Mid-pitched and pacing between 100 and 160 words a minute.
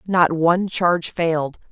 Yes: medium, 170 Hz; average, 140 wpm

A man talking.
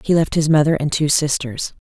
No: female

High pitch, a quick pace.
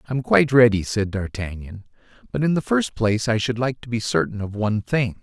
No: low, 115 Hz; fast, 230 wpm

